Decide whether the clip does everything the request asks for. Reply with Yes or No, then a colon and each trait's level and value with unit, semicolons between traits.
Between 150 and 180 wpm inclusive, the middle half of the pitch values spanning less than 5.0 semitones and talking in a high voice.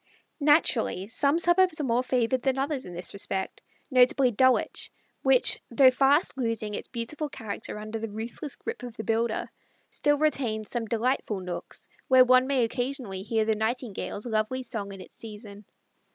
Yes: average, 165 wpm; average, 3.6 semitones; high, 240 Hz